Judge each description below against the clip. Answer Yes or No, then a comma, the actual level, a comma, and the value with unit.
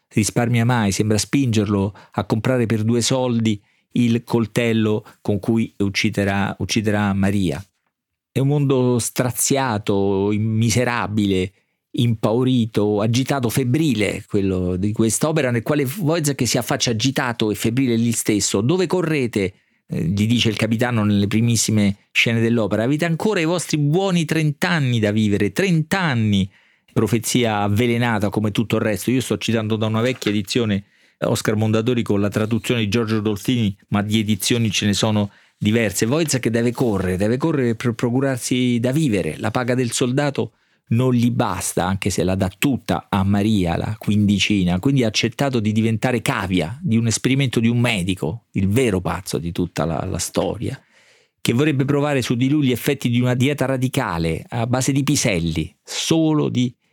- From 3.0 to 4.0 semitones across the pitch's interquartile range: Yes, average, 3.7 semitones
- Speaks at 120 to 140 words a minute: No, average, 155 wpm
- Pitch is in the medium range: No, low, 115 Hz